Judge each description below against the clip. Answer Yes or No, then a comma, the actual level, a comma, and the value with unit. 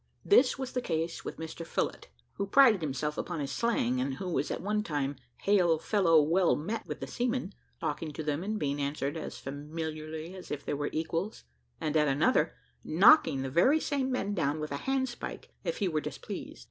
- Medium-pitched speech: Yes, medium, 165 Hz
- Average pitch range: No, wide, 5.7 semitones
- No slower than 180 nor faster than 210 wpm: Yes, average, 200 wpm